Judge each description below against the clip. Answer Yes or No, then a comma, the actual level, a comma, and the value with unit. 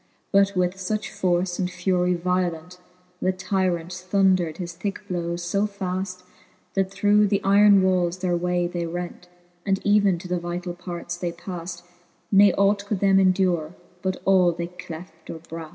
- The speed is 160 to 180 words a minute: Yes, average, 165 wpm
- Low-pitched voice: No, medium, 180 Hz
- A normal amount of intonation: No, narrow, 1.8 semitones